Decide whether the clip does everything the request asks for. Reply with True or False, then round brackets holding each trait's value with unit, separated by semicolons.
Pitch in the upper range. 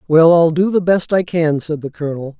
False (165 Hz)